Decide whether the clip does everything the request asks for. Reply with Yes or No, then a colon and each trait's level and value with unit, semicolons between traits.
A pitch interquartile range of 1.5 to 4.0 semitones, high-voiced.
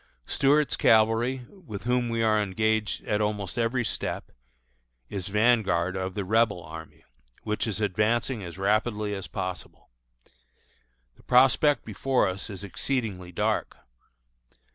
No: average, 3.5 semitones; low, 105 Hz